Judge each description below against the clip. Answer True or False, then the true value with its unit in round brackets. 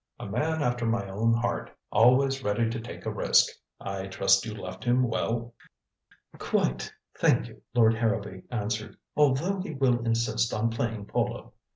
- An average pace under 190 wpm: True (160 wpm)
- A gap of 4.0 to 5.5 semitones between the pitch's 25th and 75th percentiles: False (2.5 semitones)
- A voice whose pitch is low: True (115 Hz)